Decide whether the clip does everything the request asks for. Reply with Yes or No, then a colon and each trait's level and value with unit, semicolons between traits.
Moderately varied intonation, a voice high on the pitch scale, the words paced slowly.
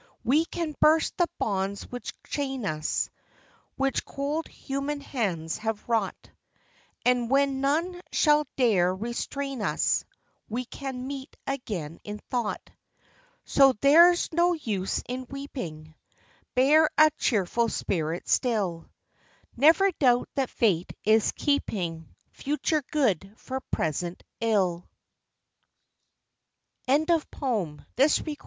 No: wide, 6.1 semitones; very high, 250 Hz; slow, 105 wpm